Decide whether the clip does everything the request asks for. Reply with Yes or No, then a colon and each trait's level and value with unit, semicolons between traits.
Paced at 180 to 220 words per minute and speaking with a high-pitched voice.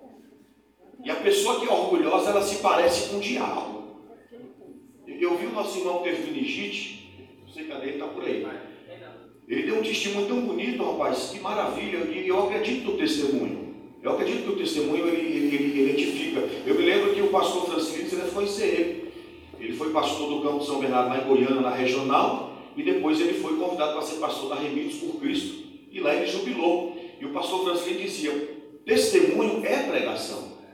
Yes: fast, 185 wpm; high, 205 Hz